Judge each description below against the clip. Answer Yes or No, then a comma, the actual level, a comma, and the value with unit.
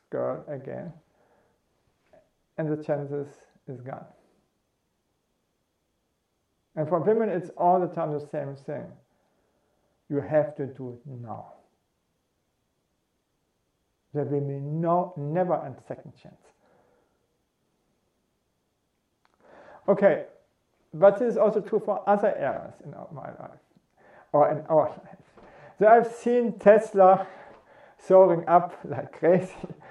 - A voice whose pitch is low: No, medium, 165 Hz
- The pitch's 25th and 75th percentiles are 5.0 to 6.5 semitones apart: Yes, average, 5.3 semitones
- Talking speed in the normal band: No, slow, 110 wpm